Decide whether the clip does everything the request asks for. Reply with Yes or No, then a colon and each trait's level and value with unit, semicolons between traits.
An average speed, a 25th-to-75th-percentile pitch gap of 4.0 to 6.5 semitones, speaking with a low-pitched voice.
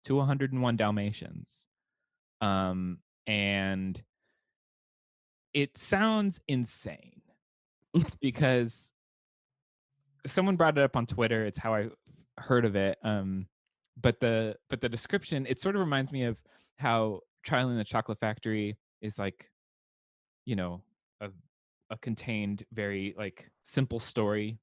No: slow, 120 wpm; average, 4.4 semitones; low, 115 Hz